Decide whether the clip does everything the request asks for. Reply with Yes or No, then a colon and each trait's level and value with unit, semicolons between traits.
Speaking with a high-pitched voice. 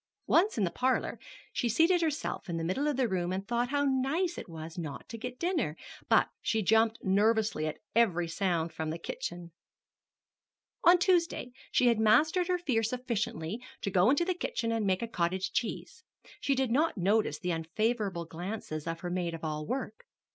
Yes: high, 220 Hz